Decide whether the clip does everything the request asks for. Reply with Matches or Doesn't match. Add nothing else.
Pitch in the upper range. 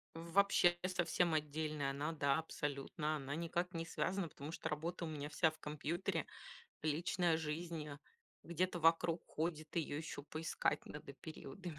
Doesn't match